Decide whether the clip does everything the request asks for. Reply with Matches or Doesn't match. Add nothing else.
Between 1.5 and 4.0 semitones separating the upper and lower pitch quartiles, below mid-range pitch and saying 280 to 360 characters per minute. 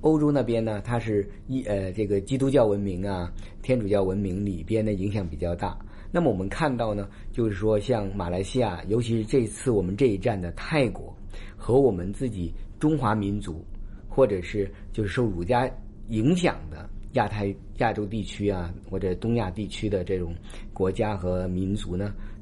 Doesn't match